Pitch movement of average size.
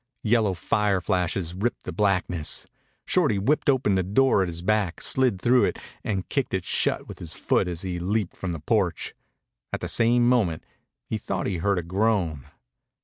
Yes: average, 4.1 semitones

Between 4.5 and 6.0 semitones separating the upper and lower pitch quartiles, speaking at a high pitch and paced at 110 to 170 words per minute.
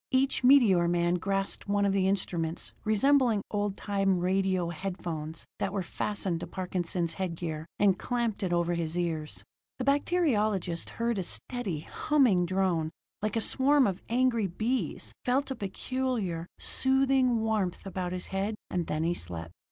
Yes: average, 5.1 semitones; high, 195 Hz; average, 160 wpm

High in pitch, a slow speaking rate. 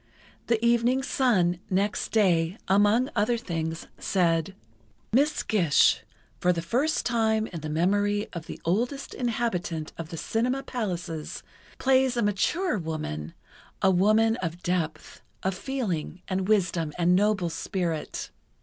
Yes: high, 195 Hz; slow, 130 wpm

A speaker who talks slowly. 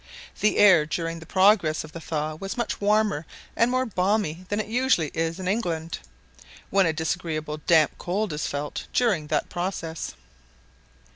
No: average, 160 wpm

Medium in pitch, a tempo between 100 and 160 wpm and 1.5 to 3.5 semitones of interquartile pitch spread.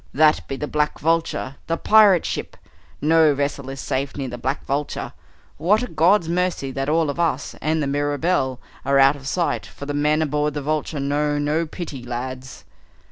No: medium, 145 Hz; average, 190 wpm; average, 2.9 semitones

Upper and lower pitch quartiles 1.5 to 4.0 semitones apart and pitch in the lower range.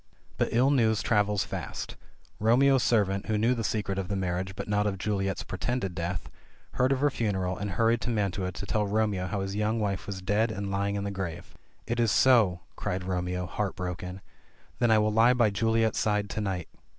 Yes: average, 2.9 semitones; low, 105 Hz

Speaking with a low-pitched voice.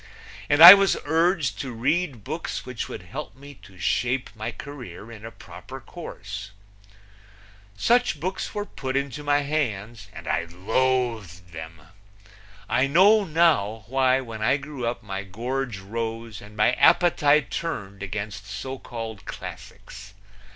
Yes: low, 120 Hz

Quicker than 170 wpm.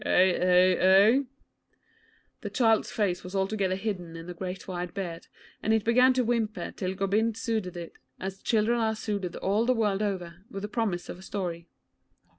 Yes: average, 180 wpm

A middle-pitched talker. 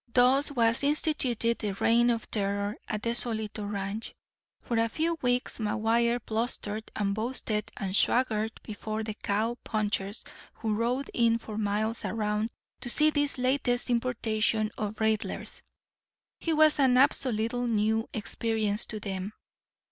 No: high, 225 Hz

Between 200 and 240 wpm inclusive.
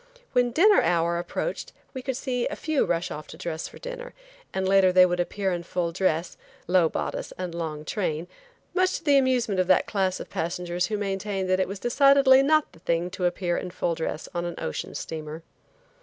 Yes: fast, 205 wpm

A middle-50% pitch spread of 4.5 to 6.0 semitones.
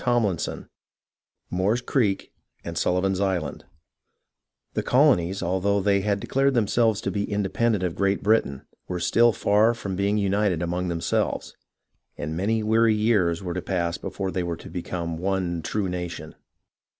No: average, 3.3 semitones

